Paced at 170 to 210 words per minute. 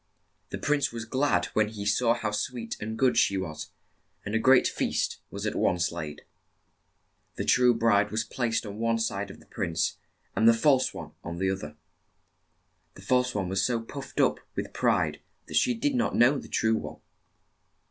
Yes: average, 190 wpm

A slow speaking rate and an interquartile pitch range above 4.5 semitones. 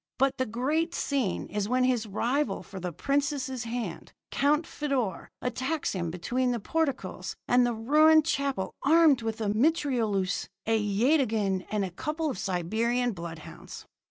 No: average, 150 wpm; wide, 5.6 semitones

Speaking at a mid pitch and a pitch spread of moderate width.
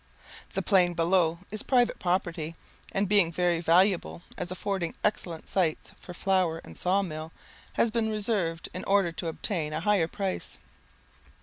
Yes: medium, 180 Hz; average, 3.1 semitones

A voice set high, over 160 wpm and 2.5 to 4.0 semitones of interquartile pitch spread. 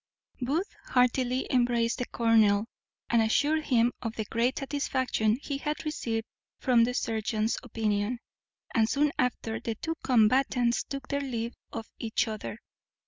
No: high, 240 Hz; average, 140 wpm; average, 2.8 semitones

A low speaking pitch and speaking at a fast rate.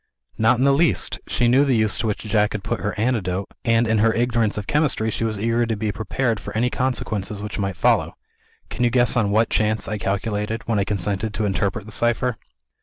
Yes: low, 110 Hz; fast, 225 wpm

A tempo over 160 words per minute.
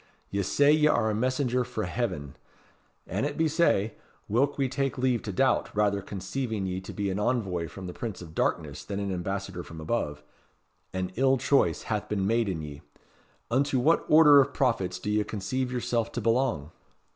Yes: average, 190 wpm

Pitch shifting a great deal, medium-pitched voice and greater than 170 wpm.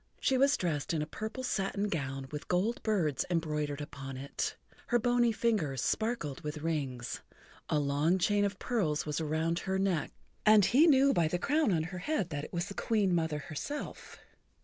Yes: wide, 6.4 semitones; medium, 175 Hz; average, 185 wpm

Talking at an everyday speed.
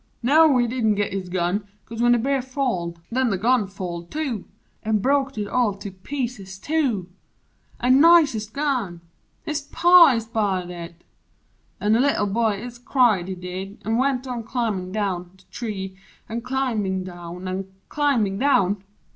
Yes: average, 165 wpm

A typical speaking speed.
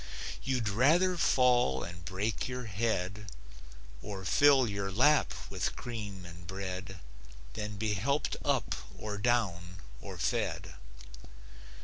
No: slow, 115 wpm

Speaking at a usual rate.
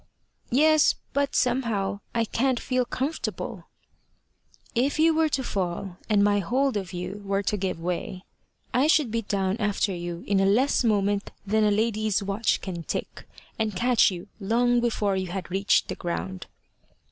Yes: average, 165 wpm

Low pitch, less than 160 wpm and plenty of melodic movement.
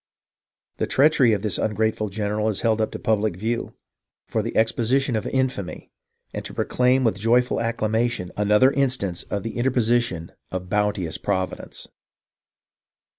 No: low, 110 Hz; average, 150 wpm; average, 2.9 semitones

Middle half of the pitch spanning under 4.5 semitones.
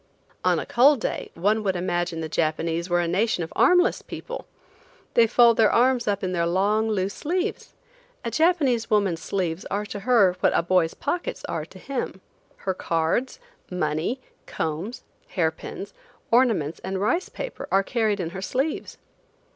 No: wide, 5.6 semitones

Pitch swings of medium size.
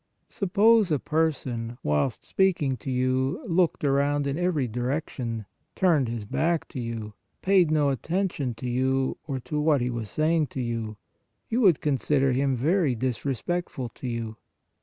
Yes: average, 4.9 semitones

